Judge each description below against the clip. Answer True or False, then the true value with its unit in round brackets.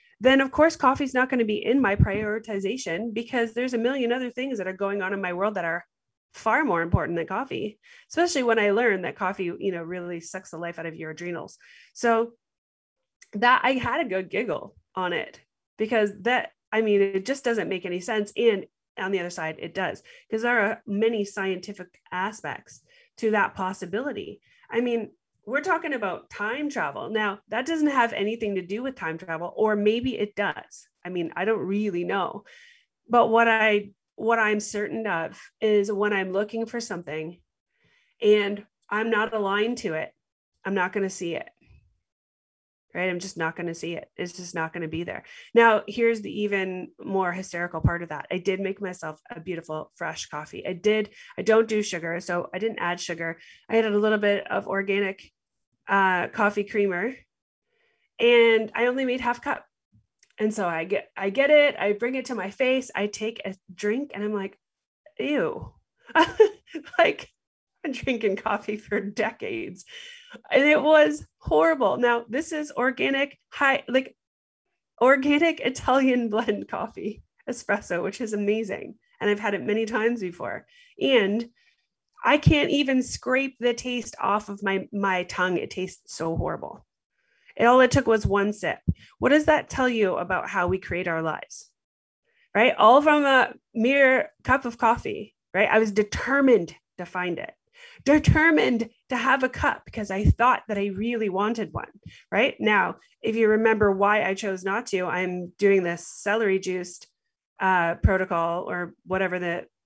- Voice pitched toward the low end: False (210 Hz)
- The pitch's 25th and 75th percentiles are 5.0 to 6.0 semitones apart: False (4.6 semitones)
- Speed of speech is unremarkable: True (180 wpm)